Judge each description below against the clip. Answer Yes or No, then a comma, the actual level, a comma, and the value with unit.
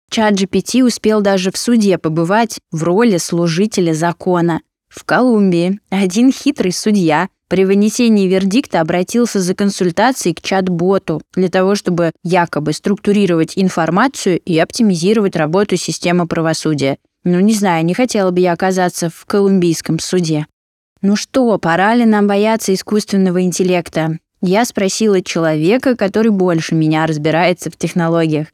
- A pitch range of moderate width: Yes, average, 3.4 semitones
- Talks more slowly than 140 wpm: Yes, average, 130 wpm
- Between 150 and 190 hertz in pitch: Yes, medium, 185 Hz